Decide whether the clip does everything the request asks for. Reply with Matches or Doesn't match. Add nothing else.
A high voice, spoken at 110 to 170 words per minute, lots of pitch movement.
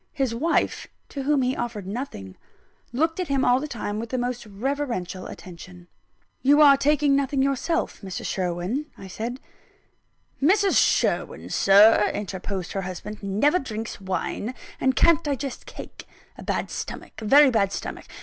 Matches